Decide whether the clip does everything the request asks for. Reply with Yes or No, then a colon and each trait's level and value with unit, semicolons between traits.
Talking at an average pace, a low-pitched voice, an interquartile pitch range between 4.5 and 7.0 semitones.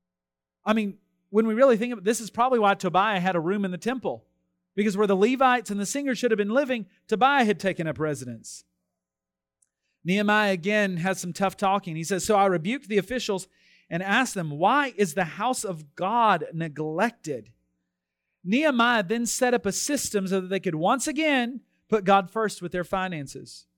No: average, 190 wpm; high, 195 Hz; average, 5.0 semitones